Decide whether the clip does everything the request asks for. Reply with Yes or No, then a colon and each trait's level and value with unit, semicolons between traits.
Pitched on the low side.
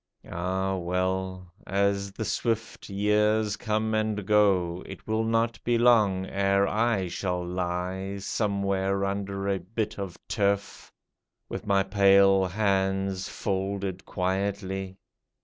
Yes: low, 100 Hz